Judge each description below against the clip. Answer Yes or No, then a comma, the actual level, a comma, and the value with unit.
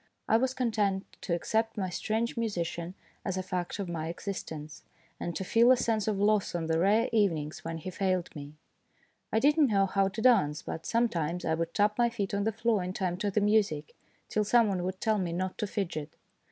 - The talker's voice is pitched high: Yes, high, 195 Hz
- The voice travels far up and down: No, average, 4.2 semitones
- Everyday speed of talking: No, fast, 220 wpm